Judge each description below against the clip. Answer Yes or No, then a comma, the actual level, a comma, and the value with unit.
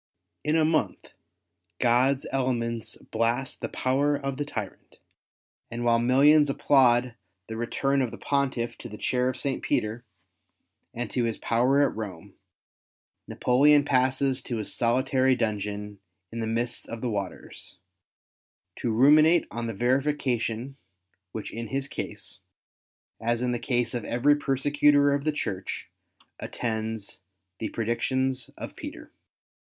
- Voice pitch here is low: Yes, low, 125 Hz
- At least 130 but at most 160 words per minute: Yes, slow, 135 wpm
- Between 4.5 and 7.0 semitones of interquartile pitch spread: No, average, 2.9 semitones